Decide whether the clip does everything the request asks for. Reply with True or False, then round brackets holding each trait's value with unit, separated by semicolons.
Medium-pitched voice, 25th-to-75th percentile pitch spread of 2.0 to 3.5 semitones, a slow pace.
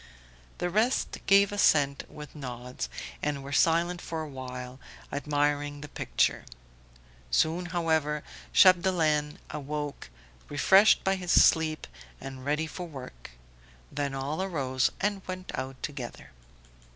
False (150 Hz; 4.0 semitones; 120 wpm)